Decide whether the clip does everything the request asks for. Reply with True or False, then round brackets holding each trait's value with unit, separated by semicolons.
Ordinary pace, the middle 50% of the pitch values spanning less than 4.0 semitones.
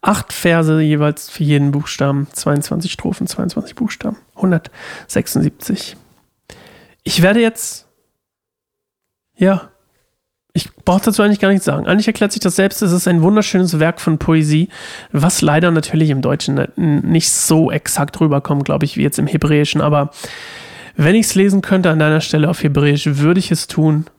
False (160 wpm; 4.3 semitones)